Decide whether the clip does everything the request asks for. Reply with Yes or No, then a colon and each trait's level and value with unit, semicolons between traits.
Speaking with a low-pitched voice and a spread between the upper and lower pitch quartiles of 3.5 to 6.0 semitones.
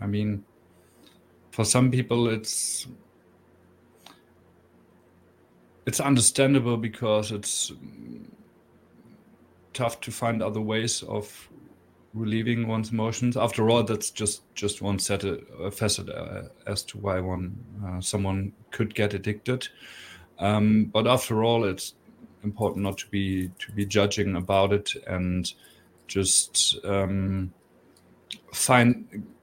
No: low, 105 Hz; average, 2.9 semitones